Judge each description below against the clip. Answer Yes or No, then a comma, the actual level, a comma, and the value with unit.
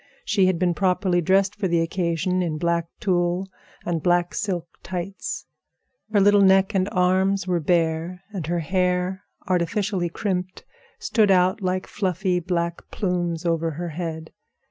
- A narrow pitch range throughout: Yes, narrow, 1.9 semitones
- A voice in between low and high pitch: Yes, medium, 180 Hz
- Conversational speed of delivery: Yes, average, 145 wpm